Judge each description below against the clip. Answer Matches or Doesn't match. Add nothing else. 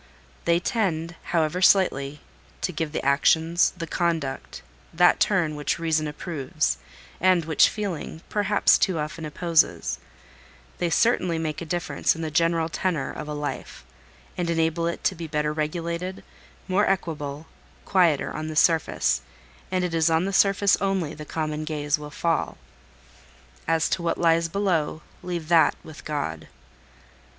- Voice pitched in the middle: Matches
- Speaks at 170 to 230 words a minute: Doesn't match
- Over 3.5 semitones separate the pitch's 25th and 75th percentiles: Doesn't match